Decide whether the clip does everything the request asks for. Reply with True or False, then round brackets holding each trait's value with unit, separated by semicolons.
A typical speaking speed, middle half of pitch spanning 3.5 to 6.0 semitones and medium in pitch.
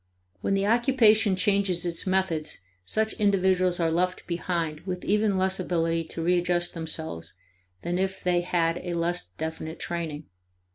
False (145 wpm; 2.4 semitones; 175 Hz)